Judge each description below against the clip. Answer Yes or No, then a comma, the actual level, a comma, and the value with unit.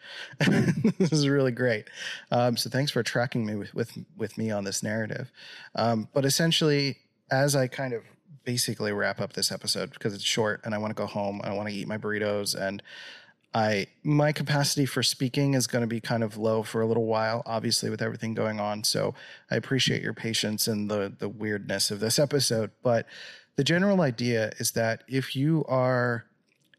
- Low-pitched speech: Yes, low, 115 Hz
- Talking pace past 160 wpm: Yes, average, 195 wpm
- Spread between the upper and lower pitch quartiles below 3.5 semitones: No, average, 4.0 semitones